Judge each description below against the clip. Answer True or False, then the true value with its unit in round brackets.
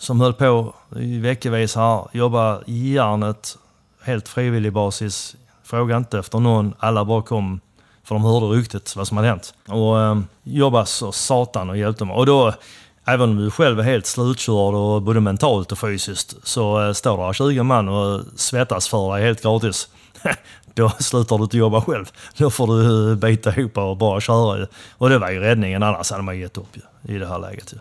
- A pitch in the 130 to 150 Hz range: False (110 Hz)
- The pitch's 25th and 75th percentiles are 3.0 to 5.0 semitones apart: False (2.6 semitones)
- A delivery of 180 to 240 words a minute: True (185 wpm)